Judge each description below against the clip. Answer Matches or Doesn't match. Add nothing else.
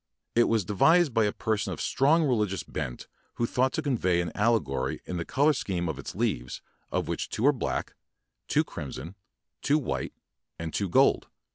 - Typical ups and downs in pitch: Doesn't match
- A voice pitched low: Matches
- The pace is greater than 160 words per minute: Matches